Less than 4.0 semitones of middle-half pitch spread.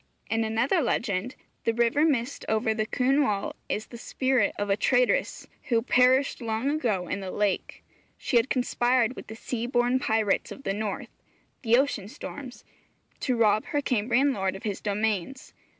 Yes: average, 3.3 semitones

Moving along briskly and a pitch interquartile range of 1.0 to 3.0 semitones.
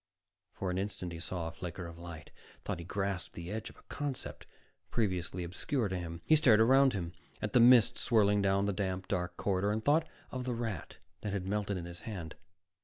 No: fast, 215 wpm; average, 4.1 semitones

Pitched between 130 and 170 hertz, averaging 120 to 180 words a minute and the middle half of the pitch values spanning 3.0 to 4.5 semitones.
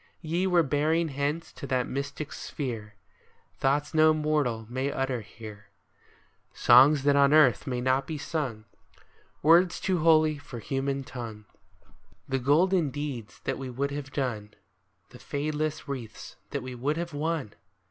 Yes: medium, 140 Hz; average, 160 wpm; average, 3.5 semitones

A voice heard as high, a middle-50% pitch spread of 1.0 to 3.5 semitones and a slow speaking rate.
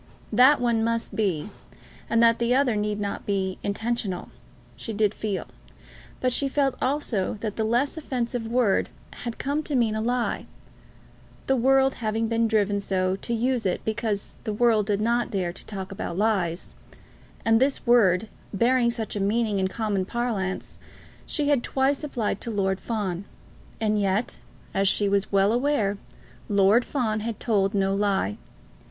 No: high, 220 Hz; average, 3.2 semitones; average, 165 wpm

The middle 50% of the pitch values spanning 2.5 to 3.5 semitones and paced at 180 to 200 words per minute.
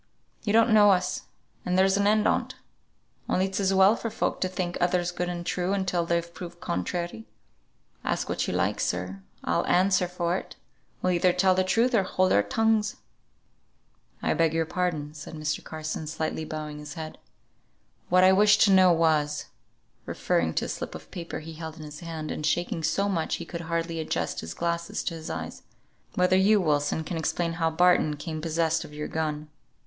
Yes: average, 2.9 semitones; average, 190 wpm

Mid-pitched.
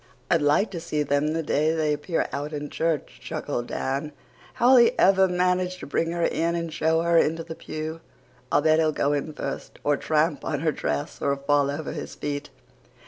Yes: medium, 155 Hz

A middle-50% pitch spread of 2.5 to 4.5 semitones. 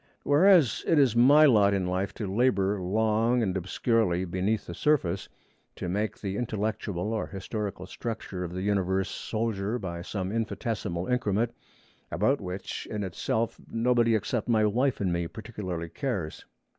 Yes: average, 3.8 semitones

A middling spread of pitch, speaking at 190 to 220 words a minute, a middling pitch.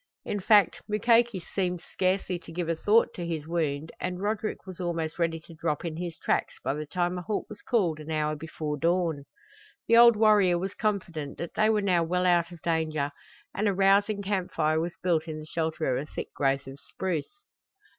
Yes: average, 3.7 semitones; fast, 205 wpm; medium, 175 Hz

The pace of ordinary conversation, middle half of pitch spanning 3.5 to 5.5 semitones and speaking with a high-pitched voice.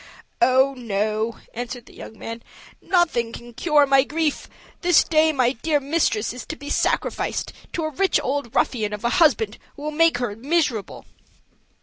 Yes: average, 165 wpm; average, 4.9 semitones; very high, 260 Hz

